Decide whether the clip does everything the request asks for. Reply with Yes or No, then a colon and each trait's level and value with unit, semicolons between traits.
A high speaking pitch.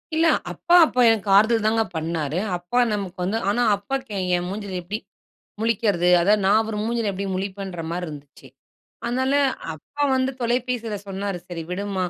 Yes: high, 205 Hz